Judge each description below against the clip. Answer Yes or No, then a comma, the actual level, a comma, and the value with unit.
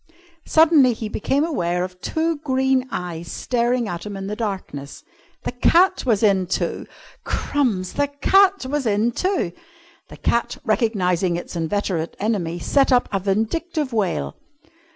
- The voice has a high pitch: Yes, high, 220 Hz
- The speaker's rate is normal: Yes, average, 145 wpm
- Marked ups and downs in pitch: Yes, wide, 7.1 semitones